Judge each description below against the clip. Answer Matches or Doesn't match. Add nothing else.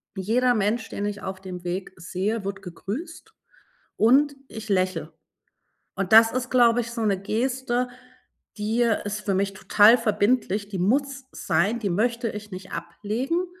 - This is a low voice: Doesn't match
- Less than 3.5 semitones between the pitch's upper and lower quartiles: Doesn't match